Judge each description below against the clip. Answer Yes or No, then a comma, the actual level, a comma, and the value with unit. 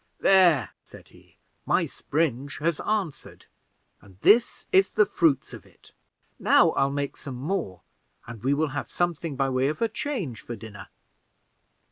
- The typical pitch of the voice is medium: Yes, medium, 145 Hz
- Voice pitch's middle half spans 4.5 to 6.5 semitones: Yes, wide, 5.6 semitones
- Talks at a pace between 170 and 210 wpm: No, average, 160 wpm